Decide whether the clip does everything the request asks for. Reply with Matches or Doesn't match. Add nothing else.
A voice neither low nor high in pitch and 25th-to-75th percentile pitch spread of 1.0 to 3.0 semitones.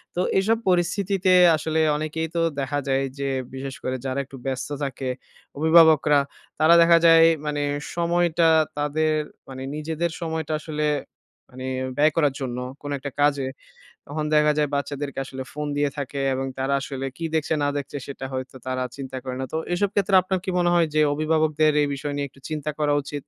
Matches